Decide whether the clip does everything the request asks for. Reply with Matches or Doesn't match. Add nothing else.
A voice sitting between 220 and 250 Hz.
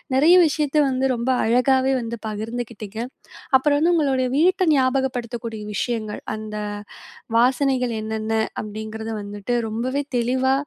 Matches